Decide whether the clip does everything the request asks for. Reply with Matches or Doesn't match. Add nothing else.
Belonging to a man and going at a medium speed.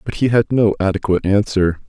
Matches